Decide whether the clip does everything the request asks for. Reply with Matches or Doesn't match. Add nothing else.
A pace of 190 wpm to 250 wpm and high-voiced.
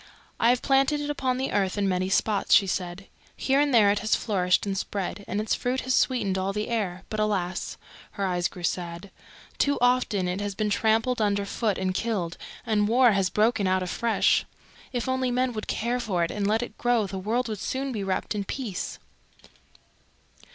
Matches